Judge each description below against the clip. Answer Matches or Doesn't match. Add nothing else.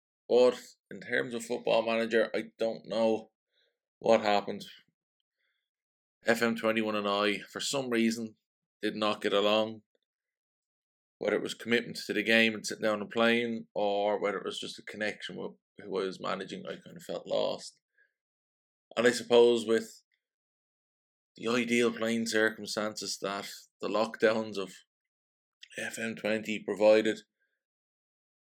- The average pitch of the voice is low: Matches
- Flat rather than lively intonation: Matches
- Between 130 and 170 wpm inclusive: Matches